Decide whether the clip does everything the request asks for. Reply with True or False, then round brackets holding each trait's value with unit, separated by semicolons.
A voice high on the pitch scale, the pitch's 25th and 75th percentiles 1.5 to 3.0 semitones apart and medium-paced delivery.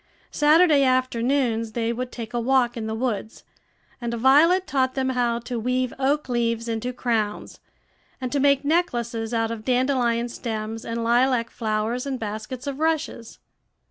True (245 Hz; 2.5 semitones; 155 wpm)